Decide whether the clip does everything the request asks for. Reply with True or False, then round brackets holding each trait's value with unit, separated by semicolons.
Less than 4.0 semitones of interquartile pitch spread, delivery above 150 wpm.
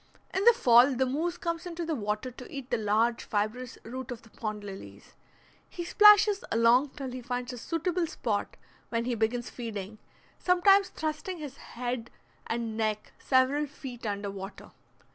False (5.6 semitones; 165 wpm)